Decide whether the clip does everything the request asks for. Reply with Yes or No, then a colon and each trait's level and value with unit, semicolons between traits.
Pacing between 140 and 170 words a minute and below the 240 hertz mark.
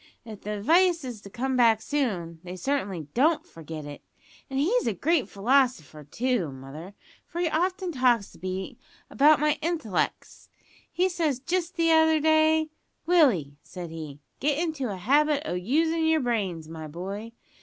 No: average, 160 wpm; very high, 255 Hz